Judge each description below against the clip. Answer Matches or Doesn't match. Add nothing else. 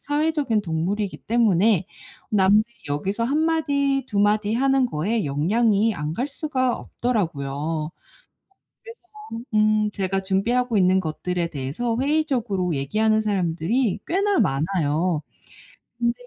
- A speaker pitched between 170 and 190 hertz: Doesn't match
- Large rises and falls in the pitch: Matches